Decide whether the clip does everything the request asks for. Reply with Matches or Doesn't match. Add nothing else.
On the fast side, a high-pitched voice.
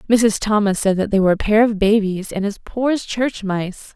Matches